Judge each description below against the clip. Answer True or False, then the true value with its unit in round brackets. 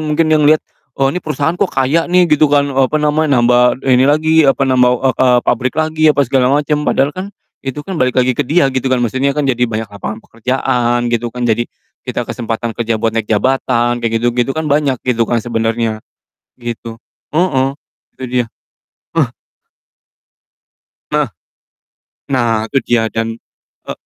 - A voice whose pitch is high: False (130 Hz)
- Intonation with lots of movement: False (3.8 semitones)